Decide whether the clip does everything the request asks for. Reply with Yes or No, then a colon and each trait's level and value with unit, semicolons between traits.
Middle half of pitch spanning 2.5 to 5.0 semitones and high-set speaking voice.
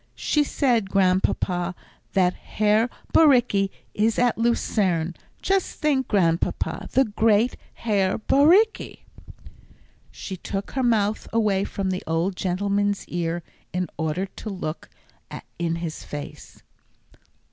Yes: average, 4.2 semitones; high, 200 Hz